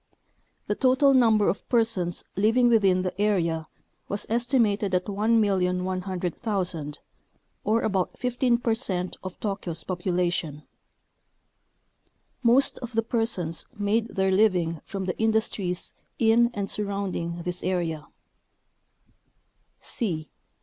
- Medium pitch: No, high, 200 Hz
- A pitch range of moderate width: Yes, average, 3.9 semitones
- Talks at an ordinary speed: No, slow, 110 wpm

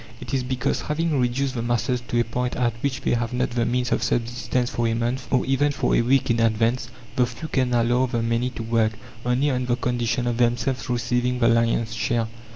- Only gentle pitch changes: Yes, narrow, 1.4 semitones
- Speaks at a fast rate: Yes, fast, 225 wpm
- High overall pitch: No, low, 120 Hz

